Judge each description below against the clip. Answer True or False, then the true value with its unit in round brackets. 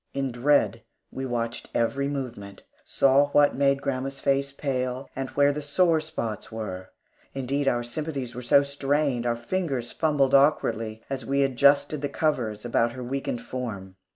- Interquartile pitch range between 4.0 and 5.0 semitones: False (2.9 semitones)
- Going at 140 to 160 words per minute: True (155 wpm)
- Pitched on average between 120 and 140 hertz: True (135 Hz)